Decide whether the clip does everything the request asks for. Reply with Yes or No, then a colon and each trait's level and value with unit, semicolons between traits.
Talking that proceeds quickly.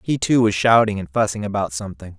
Yes: fast, 220 wpm